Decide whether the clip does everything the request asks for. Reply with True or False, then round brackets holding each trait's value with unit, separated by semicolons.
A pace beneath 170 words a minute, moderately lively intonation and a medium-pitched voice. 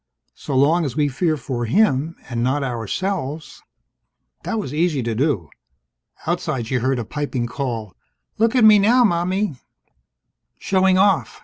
False (150 wpm; 7.0 semitones; 145 Hz)